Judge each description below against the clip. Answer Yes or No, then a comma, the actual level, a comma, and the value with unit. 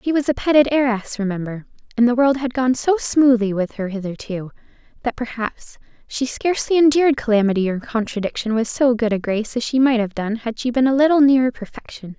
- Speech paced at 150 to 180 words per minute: No, average, 200 wpm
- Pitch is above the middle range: Yes, high, 240 Hz